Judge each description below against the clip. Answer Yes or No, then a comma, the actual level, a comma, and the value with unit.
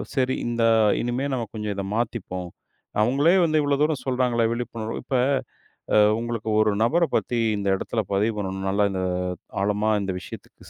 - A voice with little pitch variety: No, average, 3.6 semitones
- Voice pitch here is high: No, low, 115 Hz